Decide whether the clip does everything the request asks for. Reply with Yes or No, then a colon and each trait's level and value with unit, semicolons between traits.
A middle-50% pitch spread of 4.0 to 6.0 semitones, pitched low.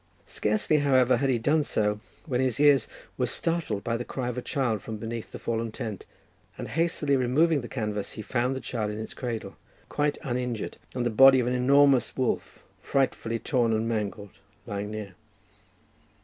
No: average, 3.6 semitones; low, 120 Hz